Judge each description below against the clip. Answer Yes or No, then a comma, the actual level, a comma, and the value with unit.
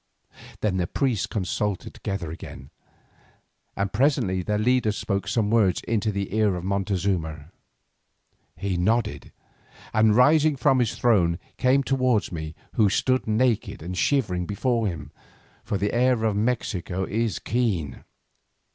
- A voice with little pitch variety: No, average, 4.5 semitones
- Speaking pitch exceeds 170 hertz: No, low, 105 Hz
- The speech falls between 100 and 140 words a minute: Yes, slow, 135 wpm